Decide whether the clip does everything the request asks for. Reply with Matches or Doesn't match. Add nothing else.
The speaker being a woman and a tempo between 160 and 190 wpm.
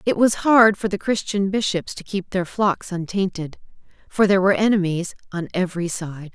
Matches